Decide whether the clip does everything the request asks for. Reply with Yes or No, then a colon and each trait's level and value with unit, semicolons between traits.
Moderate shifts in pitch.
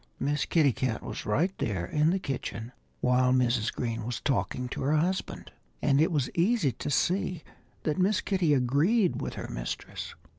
No: wide, 5.7 semitones